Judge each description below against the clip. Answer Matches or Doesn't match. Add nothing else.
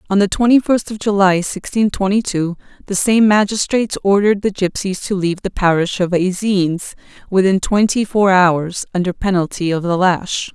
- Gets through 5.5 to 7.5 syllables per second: Doesn't match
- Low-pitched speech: Doesn't match